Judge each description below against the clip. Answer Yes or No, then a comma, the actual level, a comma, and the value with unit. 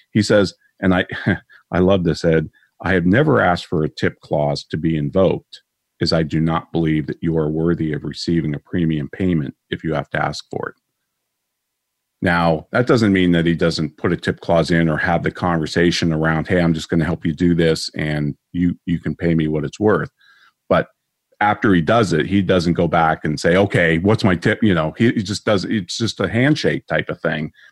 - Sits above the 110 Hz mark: No, very low, 85 Hz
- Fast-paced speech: Yes, fast, 220 wpm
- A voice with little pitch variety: No, average, 3.2 semitones